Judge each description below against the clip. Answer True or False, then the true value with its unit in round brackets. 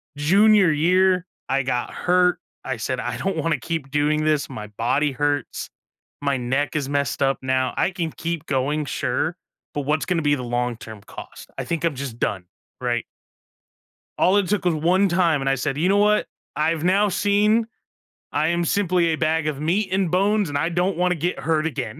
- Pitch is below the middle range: False (155 Hz)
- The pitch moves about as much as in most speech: True (4.7 semitones)